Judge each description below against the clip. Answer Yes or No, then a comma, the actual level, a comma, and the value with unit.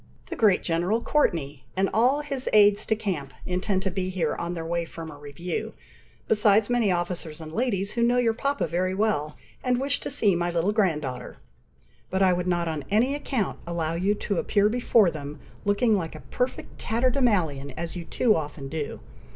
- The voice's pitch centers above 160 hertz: Yes, medium, 185 Hz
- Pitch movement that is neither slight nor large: Yes, average, 5.0 semitones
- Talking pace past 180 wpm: Yes, average, 190 wpm